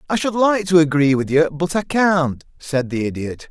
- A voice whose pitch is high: No, medium, 160 Hz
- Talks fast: Yes, fast, 220 wpm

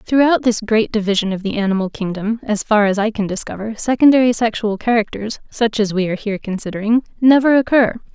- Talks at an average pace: Yes, average, 185 wpm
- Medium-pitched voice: No, high, 220 Hz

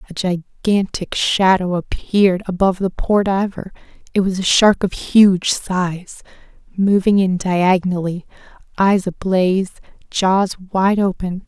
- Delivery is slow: Yes, slow, 120 wpm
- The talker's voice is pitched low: No, high, 190 Hz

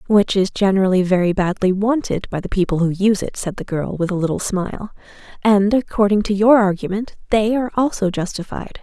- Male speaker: No, female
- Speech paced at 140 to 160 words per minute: No, average, 190 wpm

